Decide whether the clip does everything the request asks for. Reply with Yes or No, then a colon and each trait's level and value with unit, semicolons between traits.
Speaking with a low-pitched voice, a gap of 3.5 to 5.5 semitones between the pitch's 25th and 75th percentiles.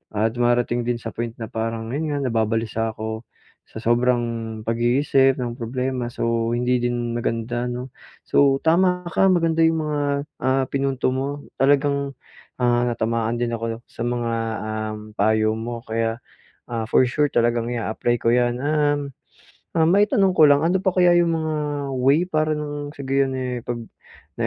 Yes: low, 120 Hz; average, 3.8 semitones